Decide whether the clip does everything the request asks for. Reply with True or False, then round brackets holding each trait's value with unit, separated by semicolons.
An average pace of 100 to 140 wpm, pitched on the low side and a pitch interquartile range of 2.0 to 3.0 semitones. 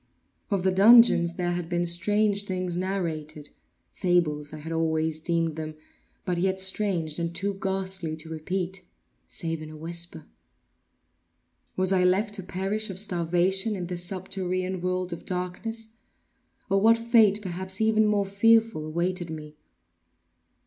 False (135 wpm; 185 Hz; 2.7 semitones)